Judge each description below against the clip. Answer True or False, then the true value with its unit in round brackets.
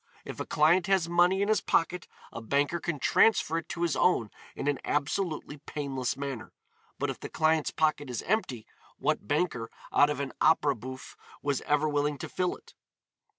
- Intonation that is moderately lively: True (3.6 semitones)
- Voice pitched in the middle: True (150 Hz)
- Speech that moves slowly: False (185 wpm)